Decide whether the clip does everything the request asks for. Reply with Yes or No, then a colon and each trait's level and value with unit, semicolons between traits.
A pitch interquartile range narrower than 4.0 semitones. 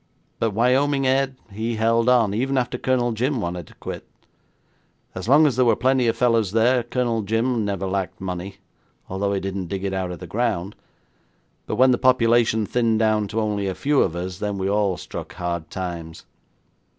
No: average, 4.3 semitones